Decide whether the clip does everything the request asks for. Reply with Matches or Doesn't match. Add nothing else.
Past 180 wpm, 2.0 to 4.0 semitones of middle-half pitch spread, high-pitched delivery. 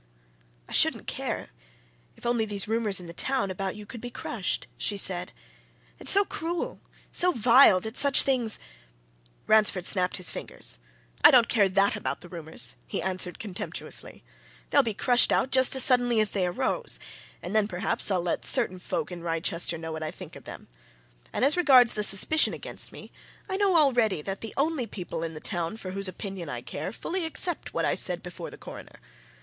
Doesn't match